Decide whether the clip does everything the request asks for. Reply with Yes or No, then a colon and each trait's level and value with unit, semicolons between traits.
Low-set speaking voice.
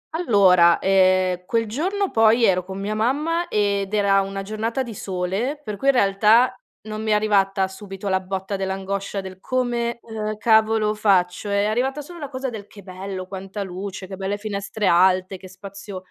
No: high, 200 Hz